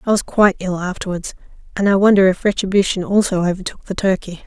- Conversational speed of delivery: Yes, average, 190 wpm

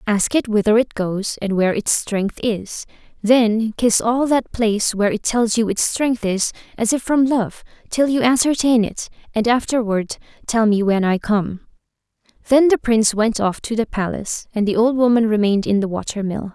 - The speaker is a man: No, female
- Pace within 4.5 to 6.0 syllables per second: Yes, 4.9 syllables/s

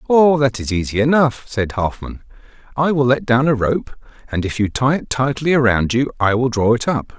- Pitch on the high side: No, low, 125 Hz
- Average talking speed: No, fast, 215 wpm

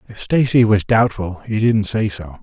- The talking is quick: Yes, fast, 220 wpm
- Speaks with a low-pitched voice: Yes, low, 105 Hz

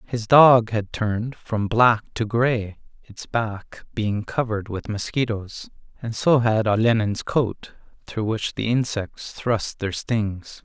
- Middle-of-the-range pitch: No, low, 110 Hz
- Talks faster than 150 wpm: No, average, 145 wpm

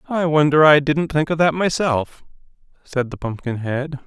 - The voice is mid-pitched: Yes, medium, 145 Hz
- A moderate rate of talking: Yes, average, 160 wpm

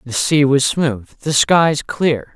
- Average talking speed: Yes, average, 180 wpm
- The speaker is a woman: No, male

